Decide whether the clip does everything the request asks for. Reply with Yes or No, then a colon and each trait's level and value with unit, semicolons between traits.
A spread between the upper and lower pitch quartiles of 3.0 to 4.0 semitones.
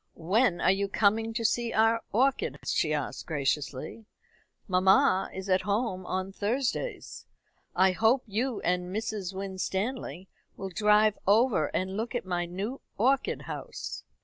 Yes: average, 3.6 semitones